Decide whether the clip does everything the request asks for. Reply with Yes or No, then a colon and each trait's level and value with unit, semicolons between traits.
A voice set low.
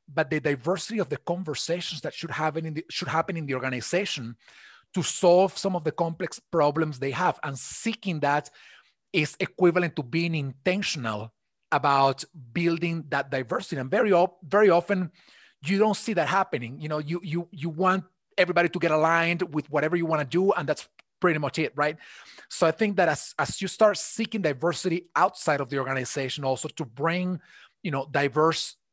No: medium, 165 Hz